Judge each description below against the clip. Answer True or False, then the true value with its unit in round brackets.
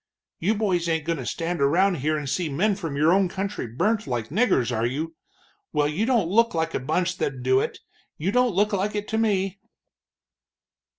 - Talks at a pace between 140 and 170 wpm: False (200 wpm)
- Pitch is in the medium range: True (175 Hz)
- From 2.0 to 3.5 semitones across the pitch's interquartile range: False (5.4 semitones)